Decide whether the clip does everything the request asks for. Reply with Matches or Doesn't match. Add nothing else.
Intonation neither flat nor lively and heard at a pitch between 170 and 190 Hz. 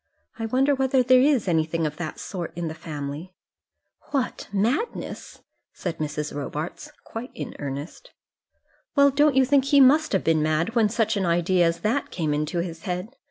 Doesn't match